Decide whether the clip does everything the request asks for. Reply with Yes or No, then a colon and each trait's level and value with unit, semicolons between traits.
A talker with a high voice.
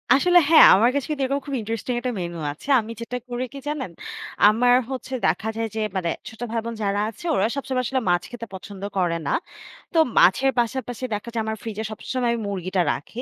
Yes: high, 230 Hz